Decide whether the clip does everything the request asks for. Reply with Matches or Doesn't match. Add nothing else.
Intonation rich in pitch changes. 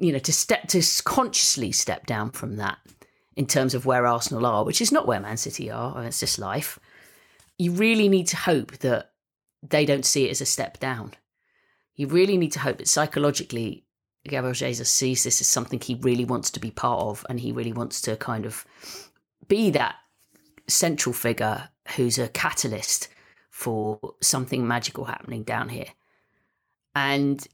Doesn't match